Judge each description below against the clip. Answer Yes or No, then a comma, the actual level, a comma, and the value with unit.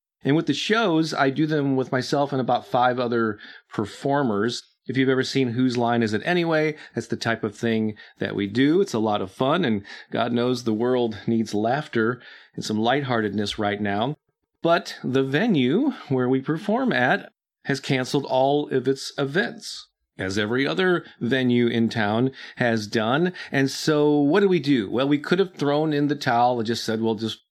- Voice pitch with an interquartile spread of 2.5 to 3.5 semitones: No, average, 4.1 semitones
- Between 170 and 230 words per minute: Yes, average, 190 wpm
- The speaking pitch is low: Yes, low, 130 Hz